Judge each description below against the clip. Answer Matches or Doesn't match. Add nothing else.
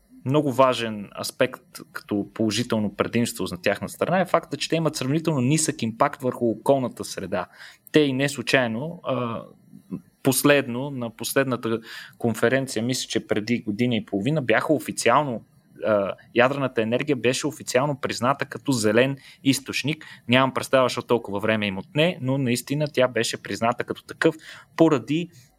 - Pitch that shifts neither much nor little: Matches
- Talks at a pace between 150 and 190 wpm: Doesn't match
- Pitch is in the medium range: Doesn't match